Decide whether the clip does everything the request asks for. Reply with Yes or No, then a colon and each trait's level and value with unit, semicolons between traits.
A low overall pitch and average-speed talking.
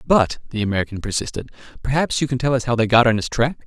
No: low, 120 Hz; fast, 245 wpm